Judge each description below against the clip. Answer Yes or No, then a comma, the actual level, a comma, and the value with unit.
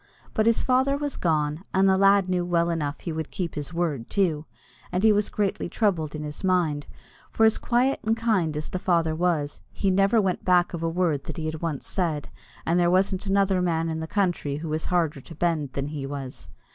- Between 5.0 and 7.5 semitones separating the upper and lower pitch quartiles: No, average, 3.9 semitones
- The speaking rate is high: Yes, fast, 230 wpm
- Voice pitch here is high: No, medium, 175 Hz